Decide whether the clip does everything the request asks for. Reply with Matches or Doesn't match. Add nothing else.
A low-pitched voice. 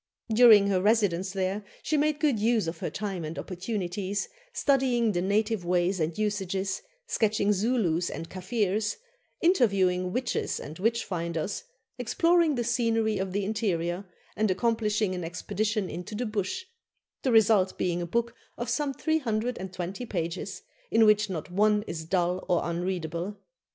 Doesn't match